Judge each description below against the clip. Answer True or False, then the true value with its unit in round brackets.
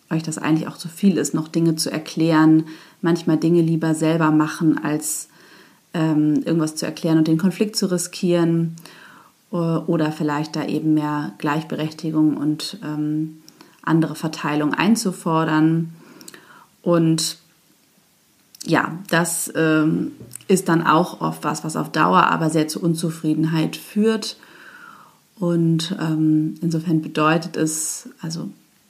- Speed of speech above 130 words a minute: False (125 wpm)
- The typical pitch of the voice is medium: True (160 Hz)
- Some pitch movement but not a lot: False (1.6 semitones)